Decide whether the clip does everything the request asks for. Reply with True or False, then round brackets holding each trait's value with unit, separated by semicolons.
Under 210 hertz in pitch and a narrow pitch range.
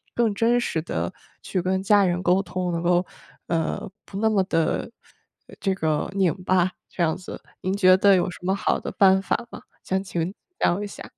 True (185 Hz; 2.0 semitones)